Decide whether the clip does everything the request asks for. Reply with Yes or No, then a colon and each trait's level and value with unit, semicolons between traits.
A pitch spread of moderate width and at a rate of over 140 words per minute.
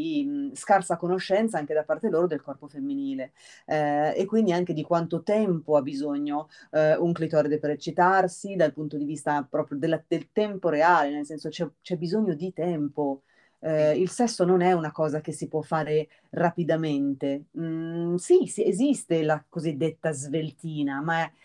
Yes: average, 3.0 semitones; fast, 170 wpm